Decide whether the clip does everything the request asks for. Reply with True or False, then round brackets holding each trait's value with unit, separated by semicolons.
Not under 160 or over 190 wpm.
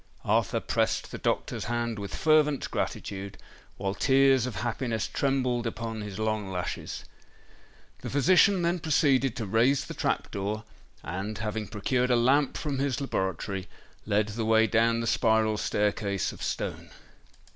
False (145 wpm)